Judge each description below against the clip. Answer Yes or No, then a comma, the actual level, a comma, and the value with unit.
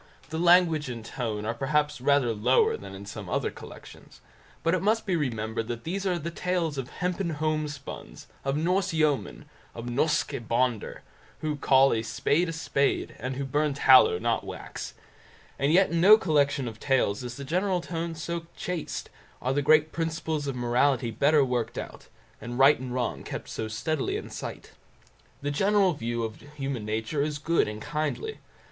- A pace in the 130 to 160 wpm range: No, average, 180 wpm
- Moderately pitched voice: Yes, medium, 145 Hz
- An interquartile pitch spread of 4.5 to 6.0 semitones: Yes, average, 5.2 semitones